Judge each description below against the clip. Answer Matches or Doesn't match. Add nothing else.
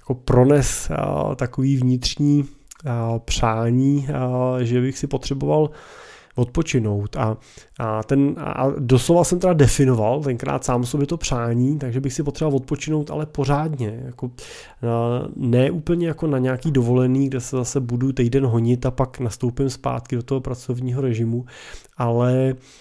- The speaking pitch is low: Matches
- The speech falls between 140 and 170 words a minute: Matches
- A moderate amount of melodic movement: Doesn't match